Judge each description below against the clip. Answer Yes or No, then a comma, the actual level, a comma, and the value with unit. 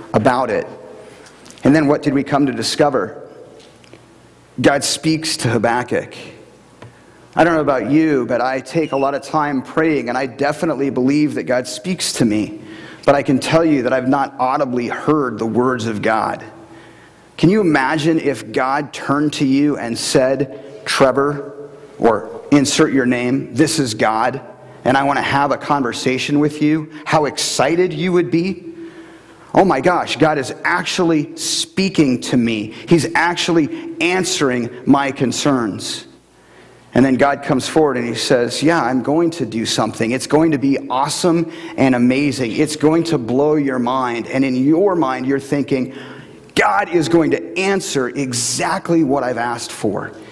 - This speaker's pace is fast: No, average, 165 wpm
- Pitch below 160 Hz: Yes, medium, 140 Hz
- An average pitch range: Yes, average, 3.8 semitones